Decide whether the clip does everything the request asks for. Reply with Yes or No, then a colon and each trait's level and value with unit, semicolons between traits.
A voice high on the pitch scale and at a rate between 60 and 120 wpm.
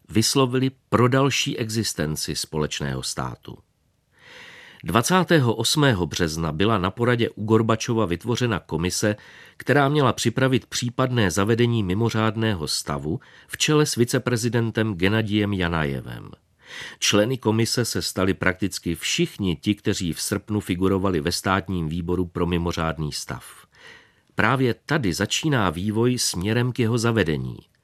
No: low, 110 Hz; slow, 115 wpm